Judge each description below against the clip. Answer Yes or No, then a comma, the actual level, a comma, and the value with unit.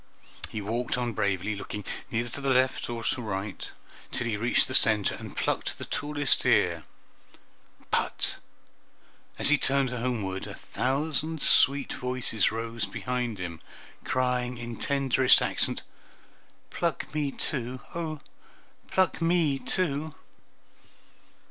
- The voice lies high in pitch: No, low, 125 Hz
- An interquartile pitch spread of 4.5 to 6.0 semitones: No, average, 3.8 semitones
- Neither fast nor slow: No, slow, 125 wpm